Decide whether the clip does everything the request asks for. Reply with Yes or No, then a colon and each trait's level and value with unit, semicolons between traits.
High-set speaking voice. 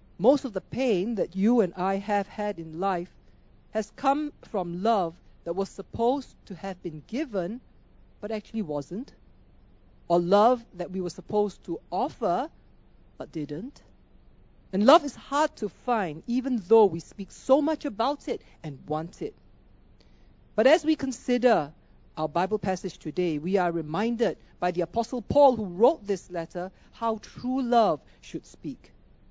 Yes: high, 205 Hz